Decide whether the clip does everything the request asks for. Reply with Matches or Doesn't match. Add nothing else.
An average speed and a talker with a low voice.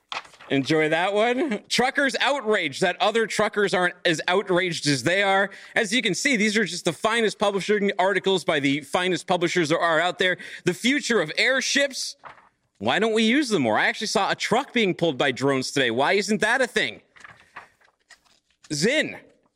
Doesn't match